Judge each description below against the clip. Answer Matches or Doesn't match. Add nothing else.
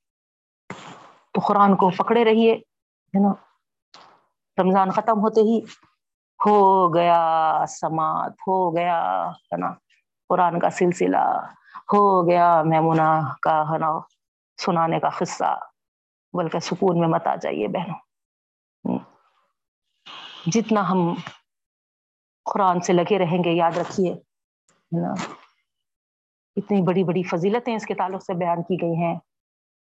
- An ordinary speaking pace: Matches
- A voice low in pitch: Doesn't match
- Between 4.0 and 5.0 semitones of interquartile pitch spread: Doesn't match